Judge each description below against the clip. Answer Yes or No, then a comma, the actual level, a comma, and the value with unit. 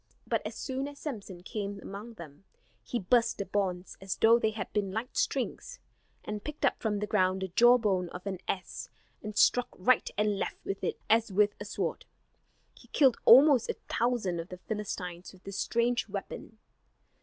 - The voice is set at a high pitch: Yes, high, 210 Hz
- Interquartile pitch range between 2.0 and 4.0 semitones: Yes, average, 3.6 semitones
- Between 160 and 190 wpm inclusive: Yes, average, 185 wpm